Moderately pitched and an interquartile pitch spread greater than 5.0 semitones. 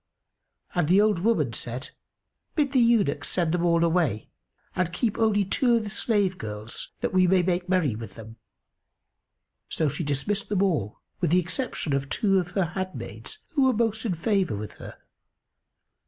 Yes: medium, 180 Hz; wide, 5.6 semitones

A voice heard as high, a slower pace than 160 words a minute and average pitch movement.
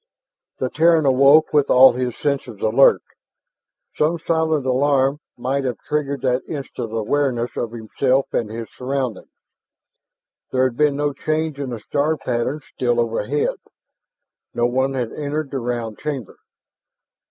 No: low, 135 Hz; average, 140 wpm; average, 3.3 semitones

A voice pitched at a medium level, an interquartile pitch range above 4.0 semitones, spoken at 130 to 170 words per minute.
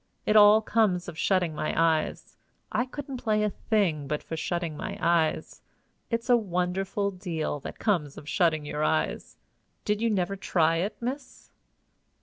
Yes: medium, 180 Hz; average, 4.8 semitones; average, 160 wpm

